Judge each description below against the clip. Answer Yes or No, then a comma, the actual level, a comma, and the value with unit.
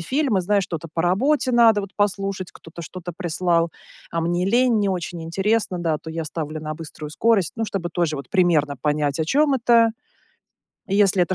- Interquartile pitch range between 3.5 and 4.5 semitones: Yes, average, 4.1 semitones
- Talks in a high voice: No, medium, 180 Hz